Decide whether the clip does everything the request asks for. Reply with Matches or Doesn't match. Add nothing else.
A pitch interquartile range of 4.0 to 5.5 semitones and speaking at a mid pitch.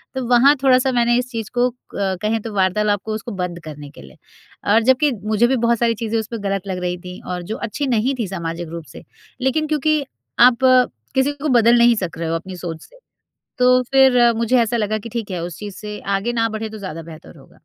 Doesn't match